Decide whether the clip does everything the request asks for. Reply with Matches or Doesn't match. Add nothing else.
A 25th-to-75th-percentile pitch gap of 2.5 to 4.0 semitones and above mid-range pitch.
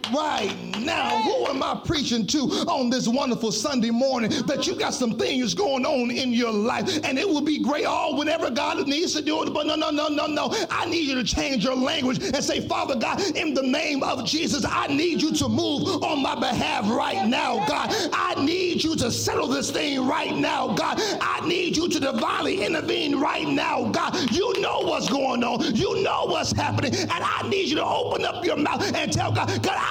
Matches